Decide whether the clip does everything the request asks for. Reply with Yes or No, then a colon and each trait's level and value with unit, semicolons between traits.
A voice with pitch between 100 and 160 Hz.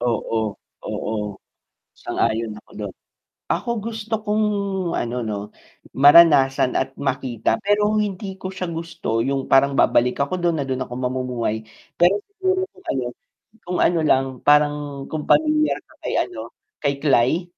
Yes: medium, 140 Hz